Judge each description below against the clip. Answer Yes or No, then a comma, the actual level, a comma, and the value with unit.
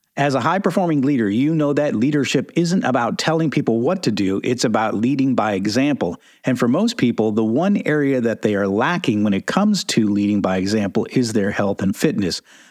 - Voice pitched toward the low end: No, medium, 145 Hz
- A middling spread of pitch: No, wide, 8.5 semitones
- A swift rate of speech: Yes, fast, 210 wpm